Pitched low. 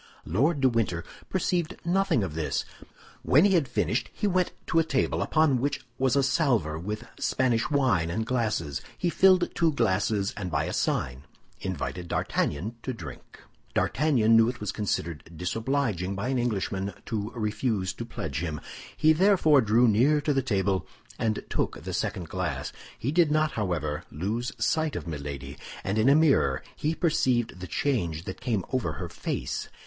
Yes: low, 115 Hz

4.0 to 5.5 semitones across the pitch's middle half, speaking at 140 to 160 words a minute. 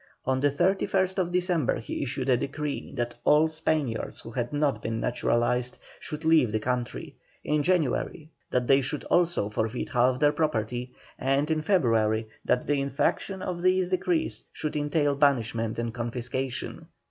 Yes: average, 4.7 semitones; average, 155 wpm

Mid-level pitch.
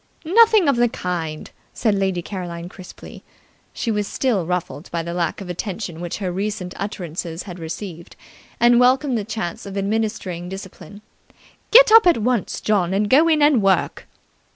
No: high, 195 Hz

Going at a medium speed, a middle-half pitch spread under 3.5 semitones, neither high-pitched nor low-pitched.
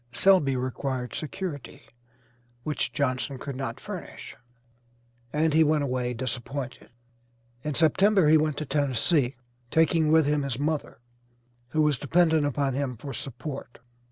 No: slow, 130 wpm; average, 3.1 semitones; medium, 145 Hz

